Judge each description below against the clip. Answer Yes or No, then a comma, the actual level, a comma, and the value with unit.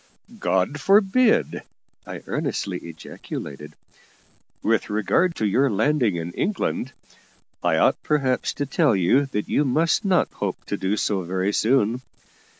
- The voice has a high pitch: No, low, 125 Hz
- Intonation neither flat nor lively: No, wide, 7.5 semitones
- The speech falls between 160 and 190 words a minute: No, slow, 135 wpm